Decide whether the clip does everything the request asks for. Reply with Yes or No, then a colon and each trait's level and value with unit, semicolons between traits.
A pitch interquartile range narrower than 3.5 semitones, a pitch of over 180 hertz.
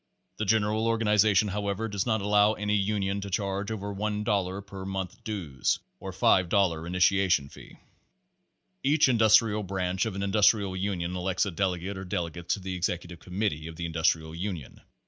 No: narrow, 2.6 semitones; very low, 95 Hz